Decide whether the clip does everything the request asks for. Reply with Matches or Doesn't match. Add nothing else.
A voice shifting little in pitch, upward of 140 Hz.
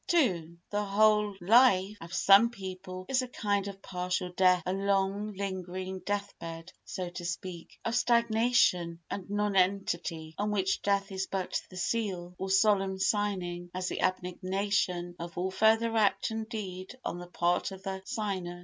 Matches